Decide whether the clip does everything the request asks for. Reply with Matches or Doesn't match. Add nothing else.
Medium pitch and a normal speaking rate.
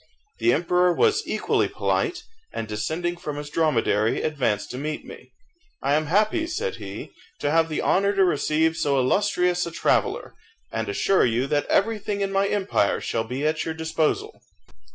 Matches